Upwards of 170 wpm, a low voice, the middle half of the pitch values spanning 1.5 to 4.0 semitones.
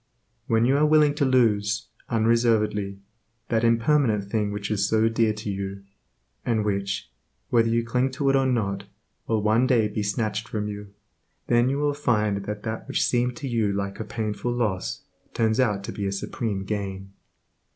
Yes: average, 180 wpm; low, 110 Hz; average, 2.8 semitones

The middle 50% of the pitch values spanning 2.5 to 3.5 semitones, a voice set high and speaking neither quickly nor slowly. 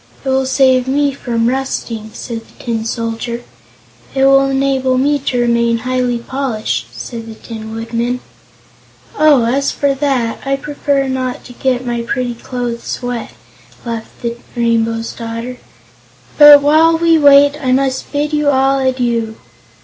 Yes: average, 2.8 semitones; very high, 255 Hz; average, 150 wpm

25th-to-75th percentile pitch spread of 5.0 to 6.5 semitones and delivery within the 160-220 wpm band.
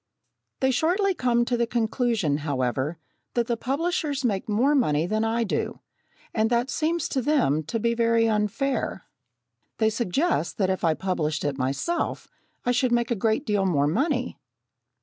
Yes: wide, 5.5 semitones; average, 165 wpm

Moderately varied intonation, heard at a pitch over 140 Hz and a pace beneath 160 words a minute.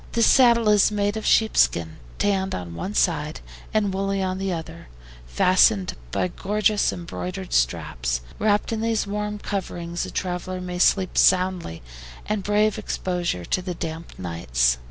Yes: average, 3.9 semitones; medium, 185 Hz; average, 150 wpm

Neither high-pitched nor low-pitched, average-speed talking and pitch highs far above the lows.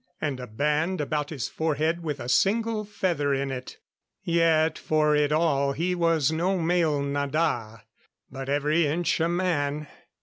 No: medium, 155 Hz; average, 155 wpm; average, 3.0 semitones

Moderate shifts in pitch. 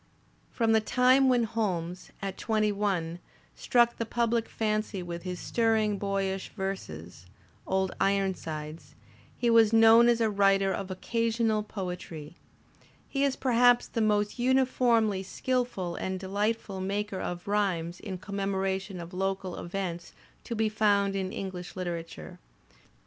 Yes: average, 3.3 semitones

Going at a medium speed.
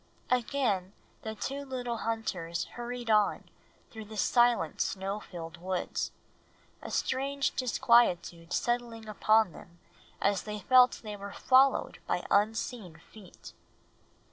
No: slow, 115 wpm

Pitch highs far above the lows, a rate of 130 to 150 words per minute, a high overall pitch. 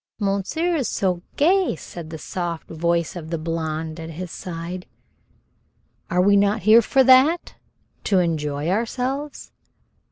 No: wide, 6.1 semitones; slow, 135 wpm; medium, 180 Hz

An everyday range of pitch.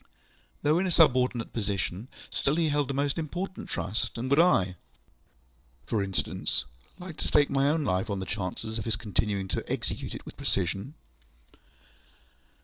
No: wide, 6.9 semitones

